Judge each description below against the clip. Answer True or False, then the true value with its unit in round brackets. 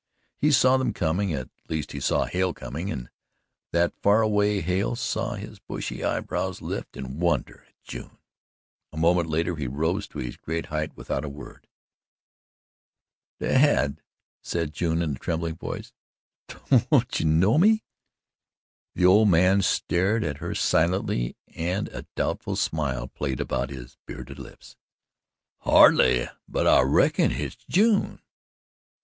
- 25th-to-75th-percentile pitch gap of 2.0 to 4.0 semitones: False (5.6 semitones)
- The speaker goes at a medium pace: True (145 wpm)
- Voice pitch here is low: True (85 Hz)